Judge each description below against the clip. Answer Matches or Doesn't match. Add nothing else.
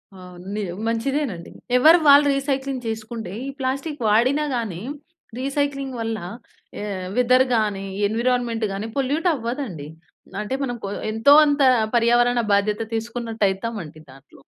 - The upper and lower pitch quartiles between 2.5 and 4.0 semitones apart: Doesn't match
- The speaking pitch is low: Doesn't match